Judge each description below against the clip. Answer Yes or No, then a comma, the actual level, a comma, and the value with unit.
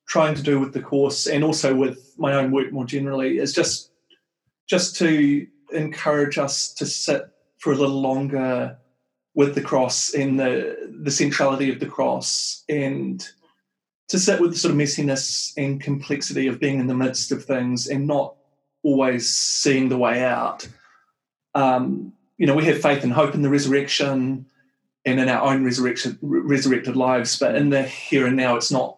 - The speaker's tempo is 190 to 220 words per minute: No, average, 180 wpm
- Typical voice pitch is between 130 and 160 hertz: Yes, medium, 140 Hz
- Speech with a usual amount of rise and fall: No, narrow, 1.9 semitones